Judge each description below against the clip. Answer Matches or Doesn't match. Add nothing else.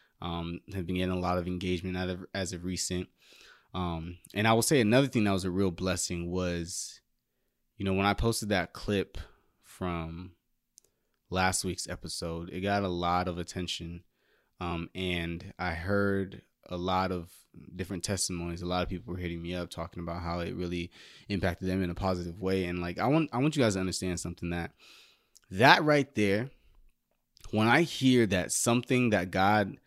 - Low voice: Matches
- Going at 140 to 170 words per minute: Doesn't match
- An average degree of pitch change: Doesn't match